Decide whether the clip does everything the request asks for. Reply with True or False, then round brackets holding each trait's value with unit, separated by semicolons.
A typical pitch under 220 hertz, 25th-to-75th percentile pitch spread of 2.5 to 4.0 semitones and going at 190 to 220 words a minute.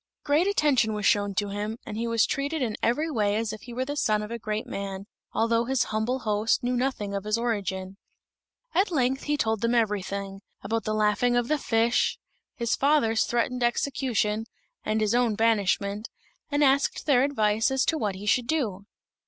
False (225 Hz; 3.5 semitones; 195 wpm)